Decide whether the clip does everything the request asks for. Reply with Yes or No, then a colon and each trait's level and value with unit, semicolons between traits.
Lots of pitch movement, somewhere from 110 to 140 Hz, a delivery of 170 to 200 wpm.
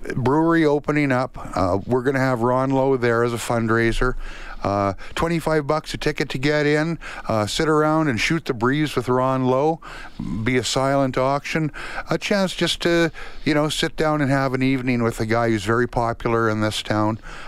No: average, 4.6 semitones; low, 135 Hz; average, 195 wpm